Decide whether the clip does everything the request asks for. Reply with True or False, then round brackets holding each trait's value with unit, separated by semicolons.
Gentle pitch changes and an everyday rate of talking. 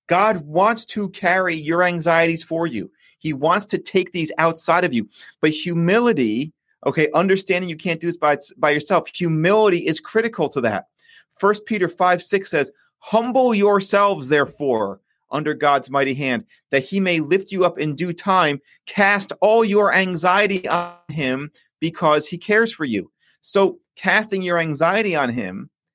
False (4.1 semitones; 160 wpm)